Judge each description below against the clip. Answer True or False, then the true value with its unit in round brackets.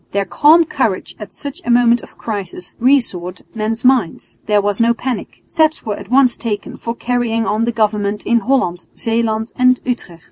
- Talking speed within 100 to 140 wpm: False (180 wpm)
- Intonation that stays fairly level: False (3.1 semitones)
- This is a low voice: False (230 Hz)